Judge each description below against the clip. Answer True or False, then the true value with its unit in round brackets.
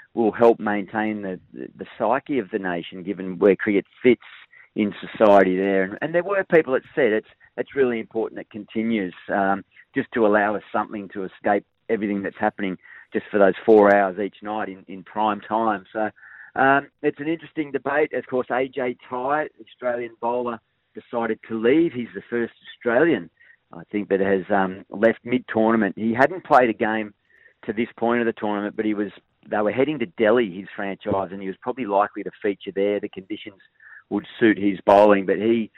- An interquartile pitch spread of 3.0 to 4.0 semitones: True (3.3 semitones)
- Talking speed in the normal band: True (195 wpm)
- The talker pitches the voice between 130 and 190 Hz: False (110 Hz)